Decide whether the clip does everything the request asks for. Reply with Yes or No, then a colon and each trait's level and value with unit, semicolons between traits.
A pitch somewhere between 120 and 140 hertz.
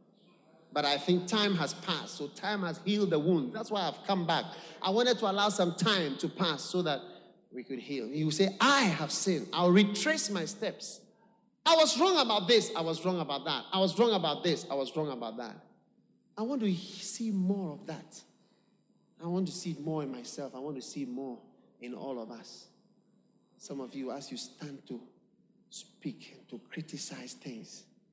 No: medium, 185 Hz